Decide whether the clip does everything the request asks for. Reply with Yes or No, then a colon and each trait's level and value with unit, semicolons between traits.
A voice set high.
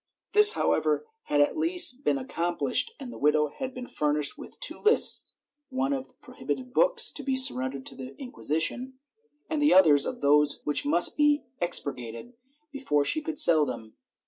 Yes: high, 245 Hz